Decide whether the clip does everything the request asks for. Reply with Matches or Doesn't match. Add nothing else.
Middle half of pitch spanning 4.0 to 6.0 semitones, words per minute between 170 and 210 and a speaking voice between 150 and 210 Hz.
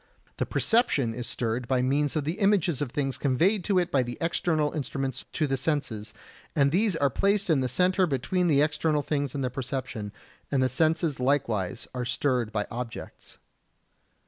Doesn't match